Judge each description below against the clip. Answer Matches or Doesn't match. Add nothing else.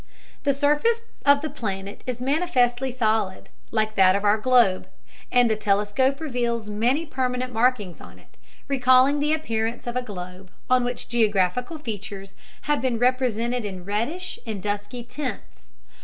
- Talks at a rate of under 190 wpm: Matches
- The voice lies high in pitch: Matches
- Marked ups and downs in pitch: Doesn't match